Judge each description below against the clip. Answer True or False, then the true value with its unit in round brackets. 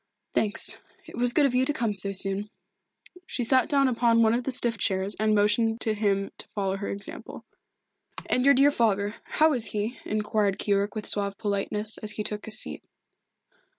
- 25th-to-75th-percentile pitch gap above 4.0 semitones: False (3.0 semitones)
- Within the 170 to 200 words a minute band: True (190 wpm)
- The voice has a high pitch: True (215 Hz)